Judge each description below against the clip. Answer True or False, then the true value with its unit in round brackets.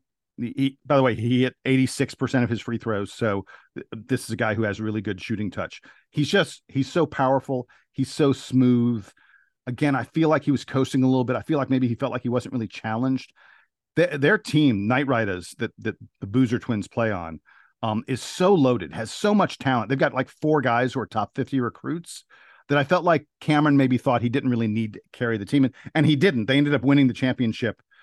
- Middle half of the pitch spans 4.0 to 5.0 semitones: False (3.4 semitones)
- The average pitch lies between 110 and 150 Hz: True (130 Hz)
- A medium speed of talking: False (230 wpm)